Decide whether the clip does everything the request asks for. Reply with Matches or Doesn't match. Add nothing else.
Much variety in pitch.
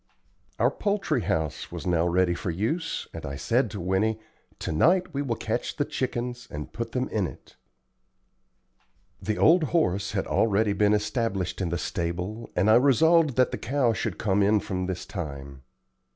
Matches